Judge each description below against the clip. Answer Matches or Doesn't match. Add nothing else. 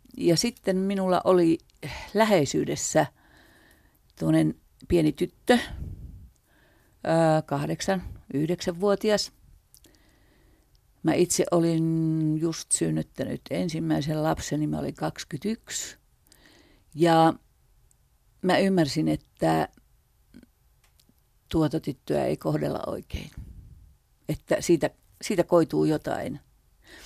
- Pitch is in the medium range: Matches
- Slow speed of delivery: Matches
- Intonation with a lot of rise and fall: Doesn't match